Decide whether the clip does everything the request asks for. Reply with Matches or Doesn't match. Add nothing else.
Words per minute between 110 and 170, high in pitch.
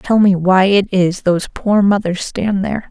Doesn't match